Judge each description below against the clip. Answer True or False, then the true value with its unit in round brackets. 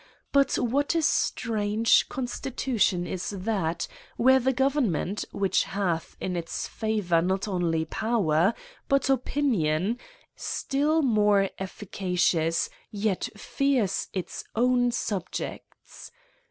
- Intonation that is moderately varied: False (5.7 semitones)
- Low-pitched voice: False (210 Hz)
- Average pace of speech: False (110 wpm)